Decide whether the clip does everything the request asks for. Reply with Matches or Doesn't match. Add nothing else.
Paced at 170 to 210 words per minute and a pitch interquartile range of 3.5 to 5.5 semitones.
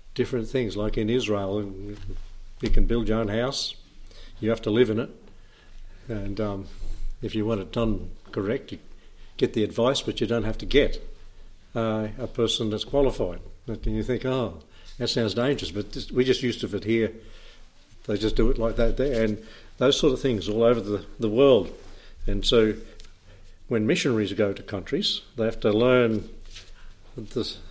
Doesn't match